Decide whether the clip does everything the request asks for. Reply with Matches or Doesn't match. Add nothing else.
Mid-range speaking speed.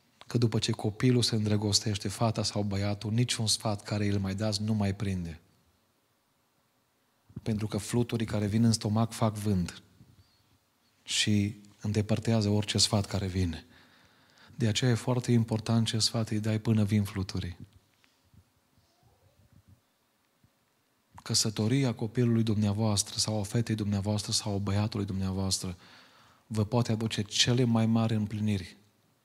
Matches